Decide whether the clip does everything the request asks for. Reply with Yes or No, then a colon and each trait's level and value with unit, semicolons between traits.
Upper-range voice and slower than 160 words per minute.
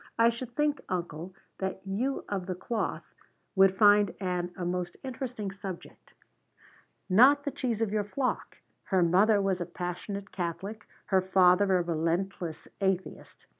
Yes: high, 195 Hz; average, 145 wpm